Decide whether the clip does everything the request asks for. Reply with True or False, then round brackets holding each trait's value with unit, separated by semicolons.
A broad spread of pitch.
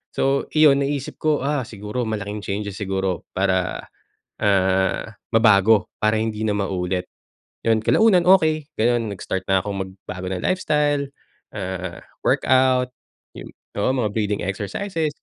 True (6.1 semitones)